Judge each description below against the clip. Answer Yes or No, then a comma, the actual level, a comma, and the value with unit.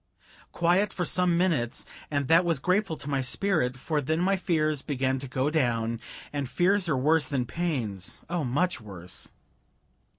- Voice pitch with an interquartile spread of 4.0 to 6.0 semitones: Yes, average, 5.3 semitones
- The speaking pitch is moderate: Yes, medium, 150 Hz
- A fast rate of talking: No, average, 165 wpm